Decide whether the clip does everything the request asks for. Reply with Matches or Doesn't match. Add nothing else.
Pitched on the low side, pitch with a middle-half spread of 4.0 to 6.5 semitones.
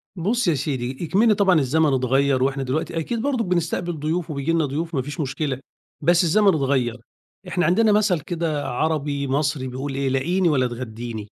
Doesn't match